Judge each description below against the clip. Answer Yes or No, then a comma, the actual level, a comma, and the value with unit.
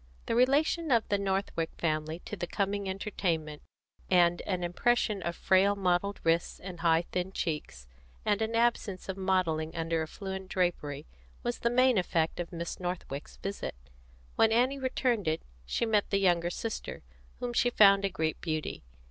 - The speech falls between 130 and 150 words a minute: No, average, 165 wpm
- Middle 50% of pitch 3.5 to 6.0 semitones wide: Yes, average, 4.0 semitones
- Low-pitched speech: No, high, 190 Hz